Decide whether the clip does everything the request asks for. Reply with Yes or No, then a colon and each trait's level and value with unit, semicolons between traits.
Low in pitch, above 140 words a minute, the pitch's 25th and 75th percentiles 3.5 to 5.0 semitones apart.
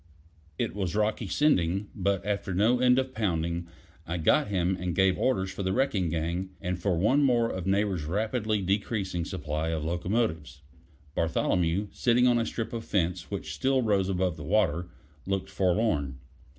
Yes: very low, 95 Hz; average, 165 wpm; average, 3.9 semitones